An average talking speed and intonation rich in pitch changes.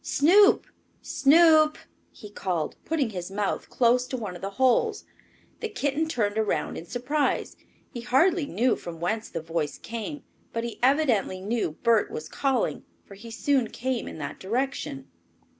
Yes: average, 160 wpm; wide, 6.2 semitones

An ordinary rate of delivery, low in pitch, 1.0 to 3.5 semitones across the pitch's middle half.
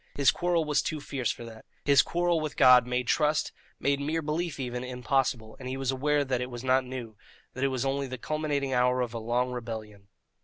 No: fast, 220 wpm; low, 130 Hz; average, 2.7 semitones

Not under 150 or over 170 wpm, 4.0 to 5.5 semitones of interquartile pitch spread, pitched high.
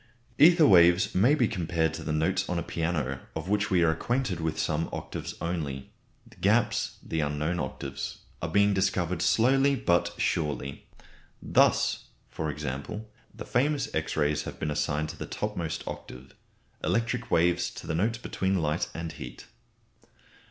No: average, 160 wpm; average, 5.0 semitones; very low, 85 Hz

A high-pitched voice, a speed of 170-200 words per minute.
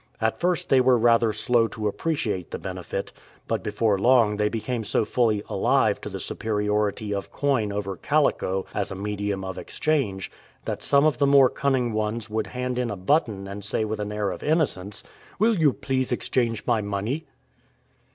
No: low, 110 Hz; average, 185 wpm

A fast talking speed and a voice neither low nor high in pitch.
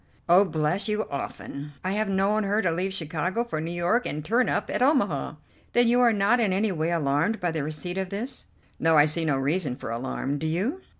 Yes: fast, 225 wpm; medium, 180 Hz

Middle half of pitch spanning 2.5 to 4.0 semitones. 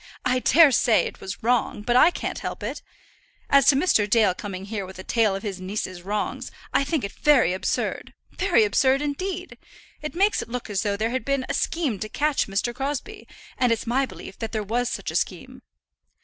No: average, 5.2 semitones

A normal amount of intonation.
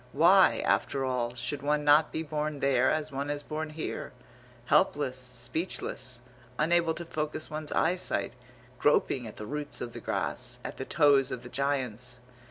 Yes: average, 3.3 semitones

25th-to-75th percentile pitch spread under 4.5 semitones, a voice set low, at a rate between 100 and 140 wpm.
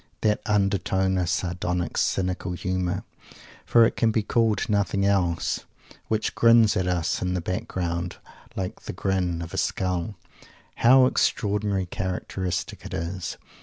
Yes: narrow, 2.6 semitones; very low, 95 Hz; slow, 135 wpm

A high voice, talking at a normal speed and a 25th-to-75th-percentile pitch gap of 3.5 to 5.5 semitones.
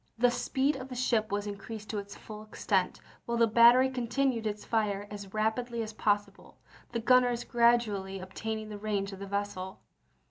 No: high, 220 Hz; average, 180 wpm; average, 2.7 semitones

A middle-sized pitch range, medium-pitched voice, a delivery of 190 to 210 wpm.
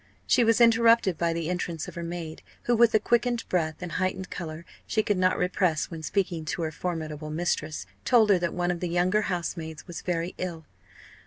Yes: average, 3.3 semitones; medium, 175 Hz; average, 200 wpm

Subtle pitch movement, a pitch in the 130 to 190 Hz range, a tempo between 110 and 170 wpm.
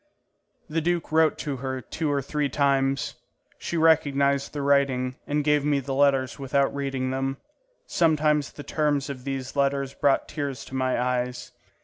Yes: narrow, 1.8 semitones; medium, 140 Hz; average, 160 wpm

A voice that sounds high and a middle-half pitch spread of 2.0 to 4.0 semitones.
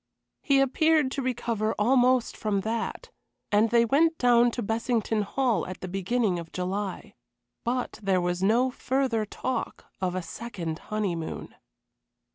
No: high, 225 Hz; average, 4.5 semitones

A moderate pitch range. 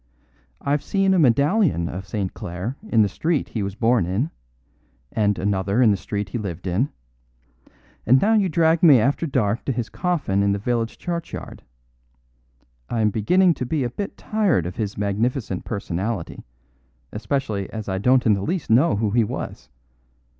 No: wide, 6.1 semitones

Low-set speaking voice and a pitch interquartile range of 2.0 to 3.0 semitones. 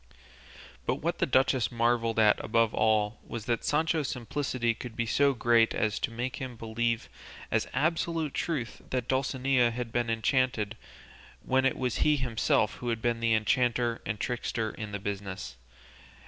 Yes: low, 120 Hz; narrow, 2.5 semitones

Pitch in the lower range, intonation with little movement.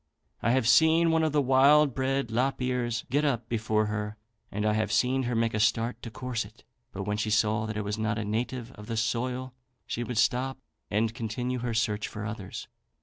No: low, 115 Hz; average, 3.1 semitones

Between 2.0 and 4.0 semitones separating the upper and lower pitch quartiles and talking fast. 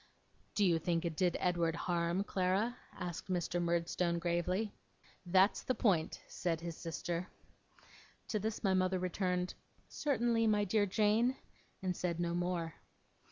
No: average, 3.1 semitones; average, 140 wpm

